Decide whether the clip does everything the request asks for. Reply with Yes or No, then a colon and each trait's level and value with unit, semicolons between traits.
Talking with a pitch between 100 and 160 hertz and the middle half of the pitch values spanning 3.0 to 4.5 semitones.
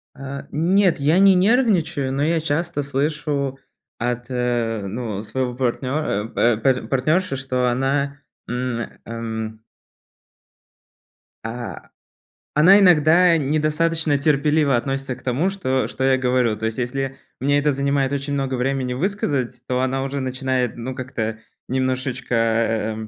Yes: low, 135 Hz; average, 3.3 semitones